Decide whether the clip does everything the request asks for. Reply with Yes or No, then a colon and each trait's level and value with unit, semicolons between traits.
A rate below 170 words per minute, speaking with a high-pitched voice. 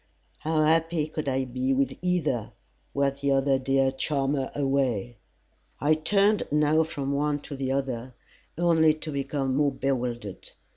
No: average, 140 wpm; medium, 140 Hz